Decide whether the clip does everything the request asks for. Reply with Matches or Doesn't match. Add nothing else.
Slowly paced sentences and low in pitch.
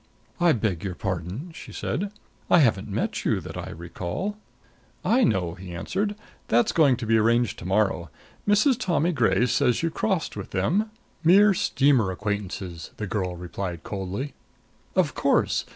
Doesn't match